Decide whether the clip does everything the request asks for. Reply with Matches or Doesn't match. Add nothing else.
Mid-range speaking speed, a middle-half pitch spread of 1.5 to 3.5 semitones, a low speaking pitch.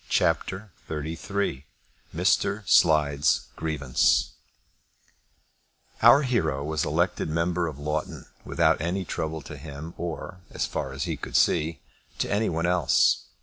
Doesn't match